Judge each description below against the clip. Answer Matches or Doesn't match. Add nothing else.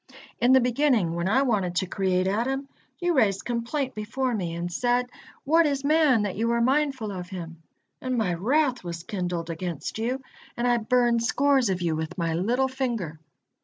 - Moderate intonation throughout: Doesn't match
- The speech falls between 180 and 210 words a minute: Matches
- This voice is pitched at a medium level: Doesn't match